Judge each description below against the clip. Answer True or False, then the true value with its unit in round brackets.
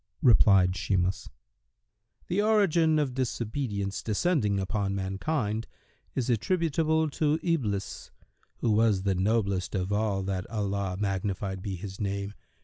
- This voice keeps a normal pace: False (120 wpm)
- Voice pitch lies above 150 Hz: False (105 Hz)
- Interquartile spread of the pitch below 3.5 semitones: False (5.5 semitones)